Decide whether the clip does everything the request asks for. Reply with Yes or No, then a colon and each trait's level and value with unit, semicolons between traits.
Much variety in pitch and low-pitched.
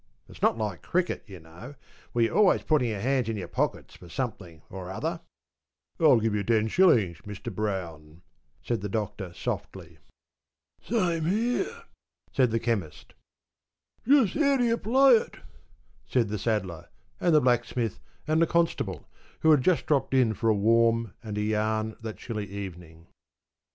Yes: wide, 7.4 semitones; low, 115 Hz